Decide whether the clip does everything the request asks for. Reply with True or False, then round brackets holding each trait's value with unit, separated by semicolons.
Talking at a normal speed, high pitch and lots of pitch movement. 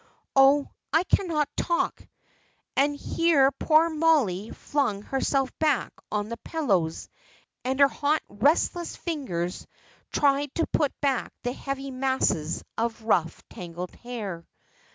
False (120 wpm; 270 Hz; 5.9 semitones)